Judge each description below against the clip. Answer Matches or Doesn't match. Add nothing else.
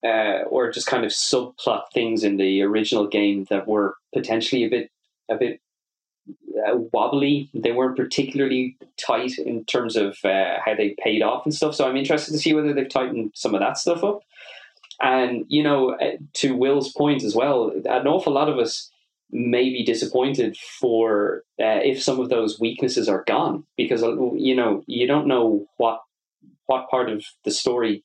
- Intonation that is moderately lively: Matches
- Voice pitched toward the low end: Matches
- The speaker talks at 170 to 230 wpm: Matches